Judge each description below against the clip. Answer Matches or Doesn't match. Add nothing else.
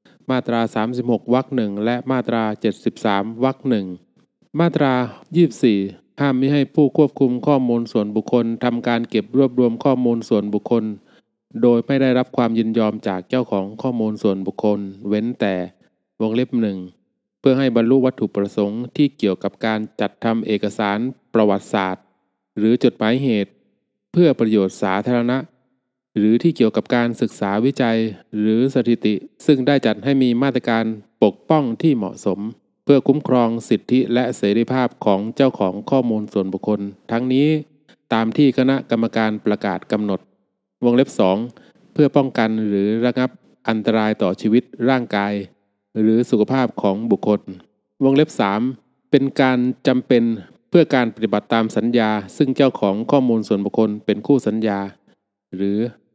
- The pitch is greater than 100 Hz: Matches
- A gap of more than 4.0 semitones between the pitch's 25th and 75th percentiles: Doesn't match